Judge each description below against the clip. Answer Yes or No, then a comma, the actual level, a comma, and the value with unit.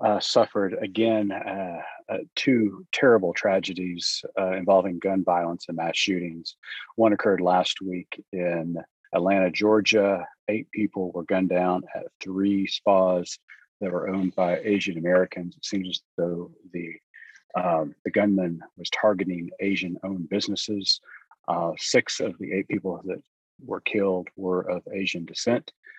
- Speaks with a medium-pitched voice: No, very low, 95 Hz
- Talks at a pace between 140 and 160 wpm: Yes, average, 145 wpm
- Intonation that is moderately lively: No, narrow, 1.8 semitones